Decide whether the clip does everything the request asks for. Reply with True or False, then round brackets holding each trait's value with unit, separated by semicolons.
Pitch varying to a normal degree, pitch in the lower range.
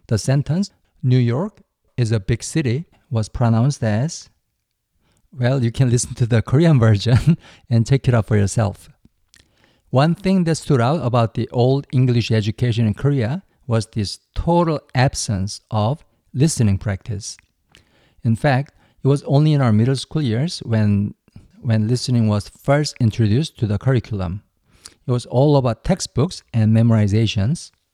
True (4.2 semitones; 120 Hz)